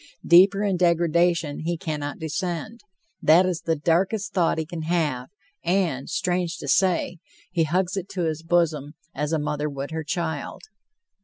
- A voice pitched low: No, medium, 170 Hz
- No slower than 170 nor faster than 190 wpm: No, average, 160 wpm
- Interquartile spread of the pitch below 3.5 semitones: Yes, average, 2.8 semitones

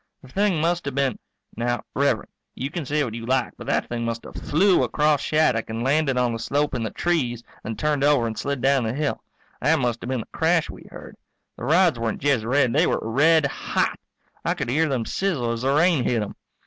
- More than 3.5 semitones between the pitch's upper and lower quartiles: Yes, average, 4.4 semitones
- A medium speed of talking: No, fast, 230 wpm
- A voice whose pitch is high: No, low, 135 Hz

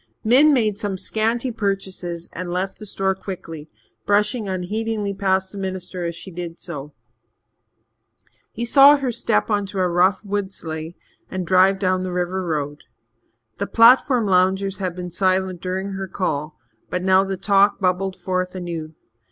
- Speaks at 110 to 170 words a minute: Yes, average, 155 wpm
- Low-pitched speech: No, high, 190 Hz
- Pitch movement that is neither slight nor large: No, narrow, 2.1 semitones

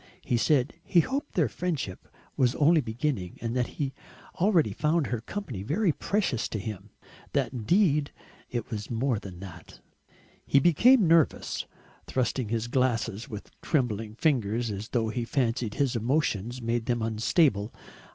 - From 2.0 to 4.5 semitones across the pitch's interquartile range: No, wide, 5.4 semitones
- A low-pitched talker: Yes, low, 120 Hz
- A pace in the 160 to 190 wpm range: No, average, 150 wpm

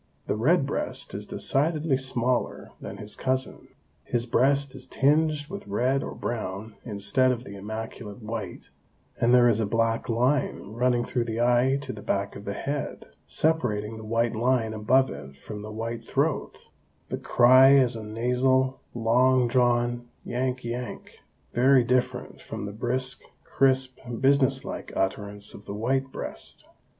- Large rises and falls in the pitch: No, average, 3.0 semitones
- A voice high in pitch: No, low, 120 Hz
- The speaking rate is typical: Yes, average, 155 wpm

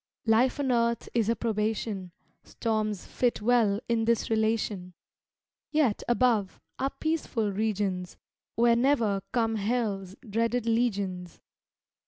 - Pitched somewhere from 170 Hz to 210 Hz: No, high, 225 Hz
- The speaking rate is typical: No, slow, 115 wpm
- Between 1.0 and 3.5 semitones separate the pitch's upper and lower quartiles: Yes, average, 2.7 semitones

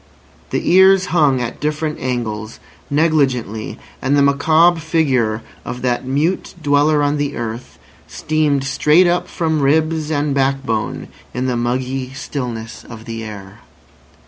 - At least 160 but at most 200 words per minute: No, slow, 135 wpm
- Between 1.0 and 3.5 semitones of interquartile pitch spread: No, average, 4.2 semitones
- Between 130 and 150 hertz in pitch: Yes, medium, 140 Hz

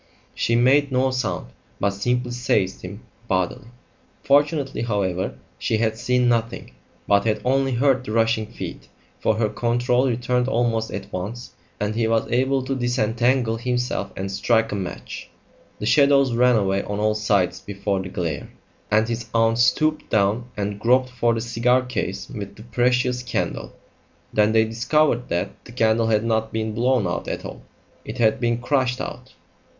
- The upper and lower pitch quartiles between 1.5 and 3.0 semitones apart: Yes, average, 2.7 semitones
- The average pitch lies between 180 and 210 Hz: No, low, 115 Hz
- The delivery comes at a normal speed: Yes, average, 165 wpm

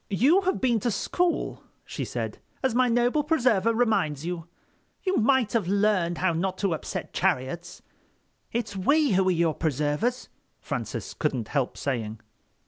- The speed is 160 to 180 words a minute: No, average, 150 wpm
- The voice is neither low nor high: No, high, 200 Hz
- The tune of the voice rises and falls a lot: Yes, wide, 6.8 semitones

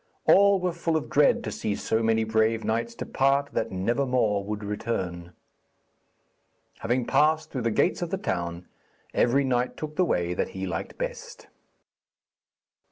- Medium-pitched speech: No, low, 115 Hz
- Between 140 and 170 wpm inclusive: Yes, average, 160 wpm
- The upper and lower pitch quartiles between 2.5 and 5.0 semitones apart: No, wide, 5.6 semitones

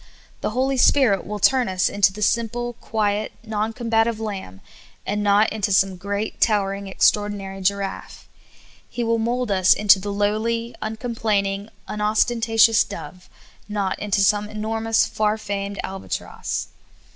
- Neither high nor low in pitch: No, high, 210 Hz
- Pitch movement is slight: Yes, narrow, 2.1 semitones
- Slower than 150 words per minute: Yes, slow, 135 wpm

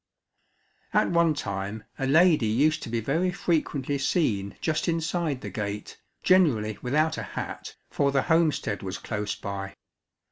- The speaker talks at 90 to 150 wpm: Yes, average, 145 wpm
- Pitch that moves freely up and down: Yes, wide, 7.3 semitones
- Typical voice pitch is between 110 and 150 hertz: Yes, medium, 140 Hz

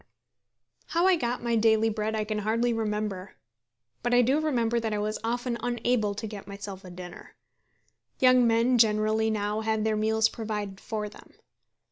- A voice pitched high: Yes, high, 220 Hz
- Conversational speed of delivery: Yes, average, 170 wpm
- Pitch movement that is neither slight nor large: No, narrow, 2.1 semitones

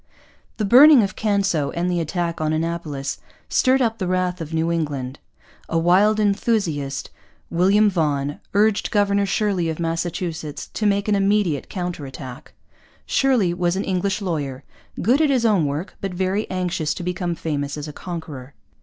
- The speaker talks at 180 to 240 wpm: No, average, 165 wpm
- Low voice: No, medium, 175 Hz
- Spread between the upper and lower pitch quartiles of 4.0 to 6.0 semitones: Yes, average, 4.4 semitones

